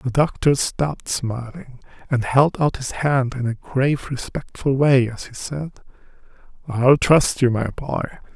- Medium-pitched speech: No, low, 130 Hz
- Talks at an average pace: Yes, average, 160 wpm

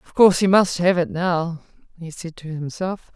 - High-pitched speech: No, medium, 175 Hz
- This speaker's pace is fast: Yes, fast, 210 wpm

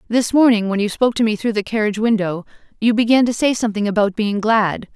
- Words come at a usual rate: No, fast, 230 wpm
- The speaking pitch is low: No, high, 220 Hz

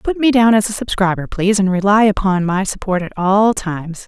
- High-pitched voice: Yes, high, 200 Hz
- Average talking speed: No, fast, 220 wpm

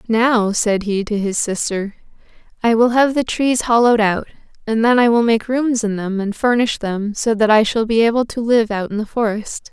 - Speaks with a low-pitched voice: No, high, 225 Hz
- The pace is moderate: No, fast, 220 wpm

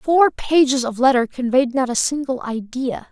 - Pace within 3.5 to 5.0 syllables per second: Yes, 4.6 syllables/s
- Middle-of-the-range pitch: No, very high, 260 Hz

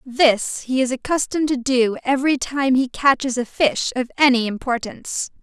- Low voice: No, very high, 260 Hz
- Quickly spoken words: No, average, 165 wpm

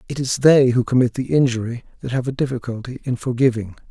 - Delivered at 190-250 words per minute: Yes, average, 200 wpm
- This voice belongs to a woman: No, male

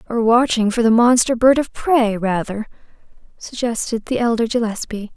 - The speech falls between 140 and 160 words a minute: Yes, average, 150 wpm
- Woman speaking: Yes, female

